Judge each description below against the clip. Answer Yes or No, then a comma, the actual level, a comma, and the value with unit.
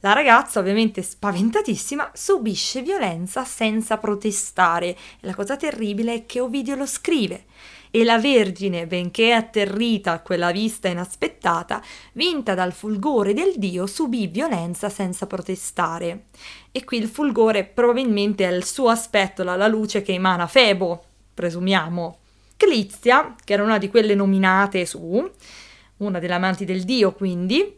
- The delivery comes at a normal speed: Yes, average, 140 wpm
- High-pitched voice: Yes, high, 205 Hz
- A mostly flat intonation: No, average, 3.7 semitones